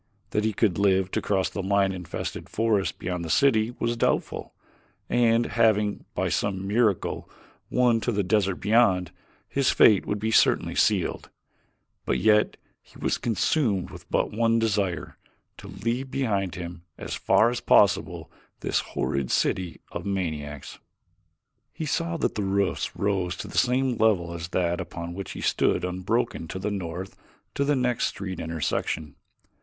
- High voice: No, low, 100 Hz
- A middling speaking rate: Yes, average, 160 wpm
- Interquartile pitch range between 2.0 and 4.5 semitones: Yes, average, 4.0 semitones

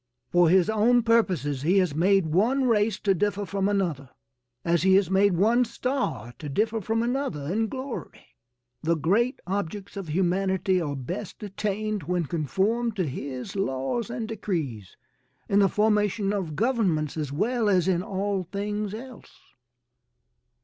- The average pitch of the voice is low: No, high, 195 Hz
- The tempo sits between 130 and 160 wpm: Yes, average, 150 wpm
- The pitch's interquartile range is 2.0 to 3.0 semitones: No, average, 4.3 semitones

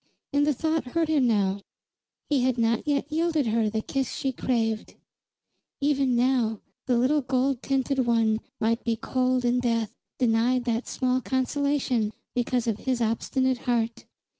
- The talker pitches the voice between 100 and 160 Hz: No, very high, 250 Hz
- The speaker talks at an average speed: Yes, average, 155 wpm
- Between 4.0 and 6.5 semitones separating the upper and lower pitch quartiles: No, average, 2.8 semitones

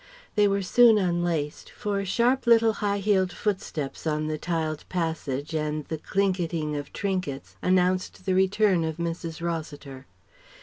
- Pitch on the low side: No, medium, 175 Hz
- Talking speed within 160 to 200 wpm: No, average, 140 wpm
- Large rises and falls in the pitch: No, average, 4.3 semitones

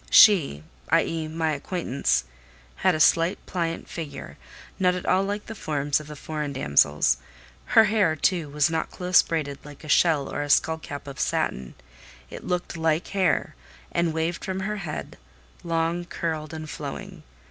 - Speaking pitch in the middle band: Yes, medium, 160 Hz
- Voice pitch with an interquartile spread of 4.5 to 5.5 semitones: No, average, 3.3 semitones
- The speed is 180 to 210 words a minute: No, average, 165 wpm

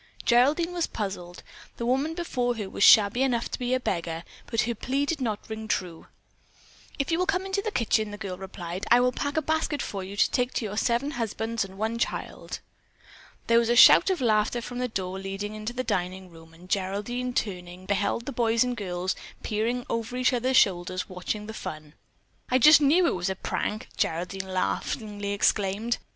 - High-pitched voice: Yes, high, 220 Hz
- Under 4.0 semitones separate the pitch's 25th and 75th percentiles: No, average, 4.6 semitones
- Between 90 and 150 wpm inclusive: No, average, 200 wpm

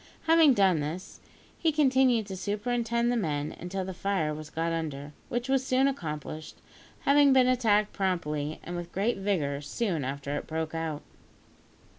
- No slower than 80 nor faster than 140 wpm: No, average, 160 wpm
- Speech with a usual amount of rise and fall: No, wide, 7.8 semitones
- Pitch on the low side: No, high, 190 Hz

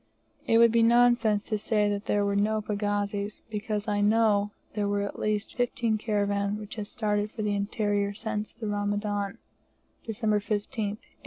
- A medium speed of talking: Yes, average, 165 wpm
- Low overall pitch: No, high, 210 Hz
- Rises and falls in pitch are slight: Yes, narrow, 1.1 semitones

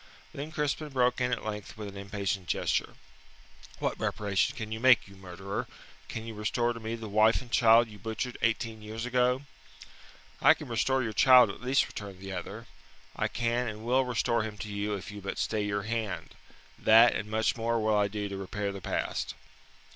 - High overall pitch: No, low, 110 Hz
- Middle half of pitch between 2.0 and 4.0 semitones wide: Yes, narrow, 2.6 semitones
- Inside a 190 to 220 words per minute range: Yes, average, 200 wpm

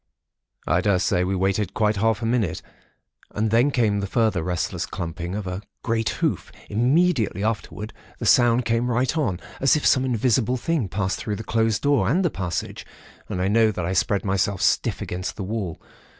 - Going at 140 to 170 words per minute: No, average, 185 wpm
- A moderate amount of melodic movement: Yes, average, 3.9 semitones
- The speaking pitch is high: No, low, 105 Hz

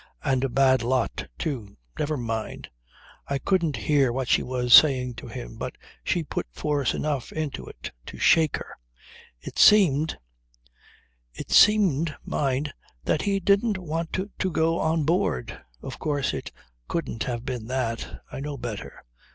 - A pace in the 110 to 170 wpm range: Yes, average, 150 wpm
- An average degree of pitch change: Yes, average, 4.4 semitones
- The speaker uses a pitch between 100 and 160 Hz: Yes, medium, 140 Hz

